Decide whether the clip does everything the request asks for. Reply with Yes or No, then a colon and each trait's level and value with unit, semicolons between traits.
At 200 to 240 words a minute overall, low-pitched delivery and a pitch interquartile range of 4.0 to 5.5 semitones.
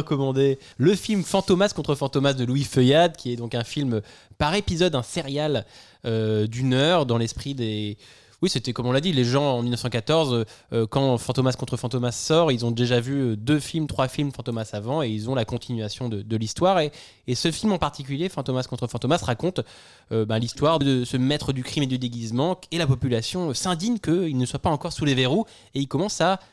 Yes: average, 215 wpm; low, 130 Hz; average, 4.4 semitones